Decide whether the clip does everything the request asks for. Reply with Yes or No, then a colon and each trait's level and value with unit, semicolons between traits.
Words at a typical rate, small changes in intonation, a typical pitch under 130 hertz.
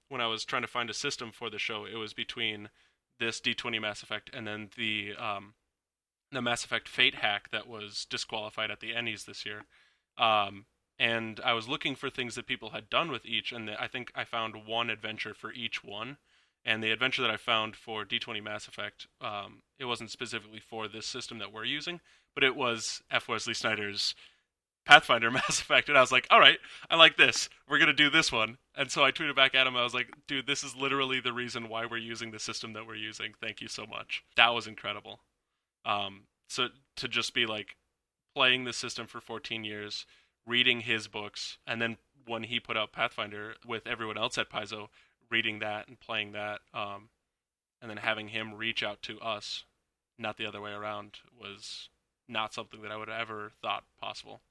No: fast, 210 wpm; narrow, 2.1 semitones; low, 115 Hz